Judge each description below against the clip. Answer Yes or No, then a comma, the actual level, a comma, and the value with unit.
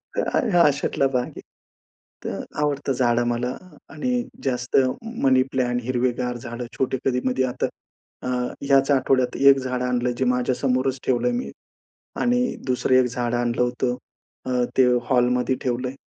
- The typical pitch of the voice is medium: No, low, 125 Hz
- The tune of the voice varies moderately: No, narrow, 1.5 semitones